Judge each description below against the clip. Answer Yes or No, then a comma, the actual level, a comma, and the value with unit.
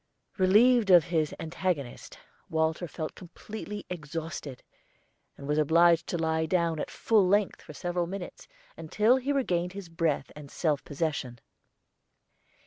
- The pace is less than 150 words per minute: Yes, slow, 135 wpm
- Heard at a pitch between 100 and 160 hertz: No, medium, 170 Hz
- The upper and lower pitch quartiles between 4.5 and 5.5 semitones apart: No, average, 3.1 semitones